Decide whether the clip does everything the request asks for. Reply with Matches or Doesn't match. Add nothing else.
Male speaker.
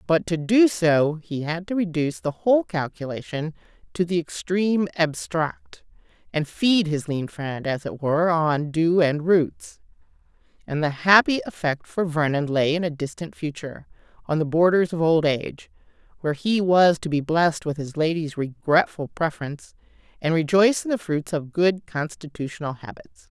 Doesn't match